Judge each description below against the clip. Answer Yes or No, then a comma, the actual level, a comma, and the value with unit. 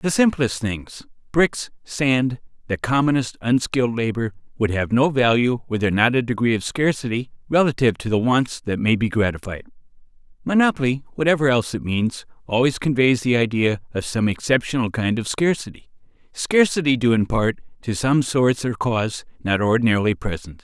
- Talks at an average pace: Yes, average, 155 wpm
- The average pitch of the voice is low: Yes, low, 120 Hz